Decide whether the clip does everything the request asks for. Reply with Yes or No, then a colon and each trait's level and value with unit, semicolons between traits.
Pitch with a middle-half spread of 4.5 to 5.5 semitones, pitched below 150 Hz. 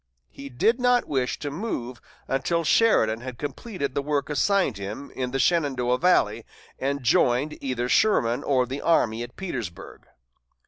Yes: average, 5.0 semitones; low, 135 Hz